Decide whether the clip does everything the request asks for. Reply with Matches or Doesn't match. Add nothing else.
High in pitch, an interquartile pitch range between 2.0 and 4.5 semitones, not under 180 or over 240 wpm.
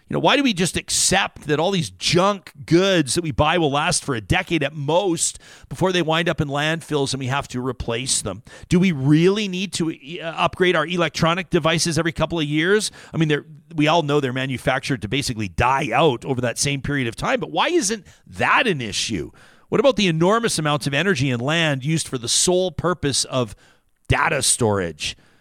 Doesn't match